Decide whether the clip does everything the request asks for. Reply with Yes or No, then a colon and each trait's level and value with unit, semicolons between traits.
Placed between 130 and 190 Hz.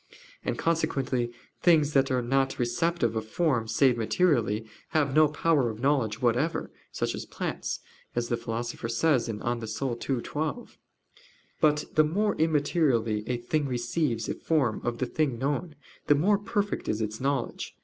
Yes: low, 135 Hz